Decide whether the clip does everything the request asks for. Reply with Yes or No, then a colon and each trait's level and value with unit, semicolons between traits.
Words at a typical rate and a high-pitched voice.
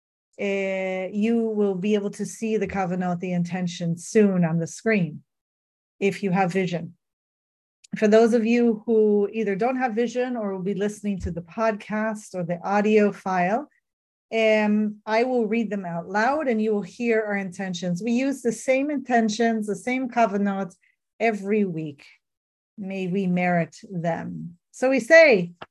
Yes: average, 165 wpm; high, 205 Hz